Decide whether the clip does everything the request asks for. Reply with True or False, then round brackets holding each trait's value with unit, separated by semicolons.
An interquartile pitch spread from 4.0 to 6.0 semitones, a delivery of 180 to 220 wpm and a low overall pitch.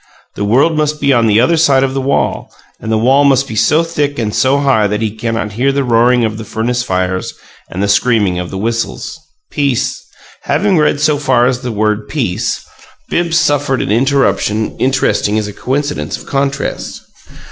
True (4.4 semitones; 190 wpm; 125 Hz)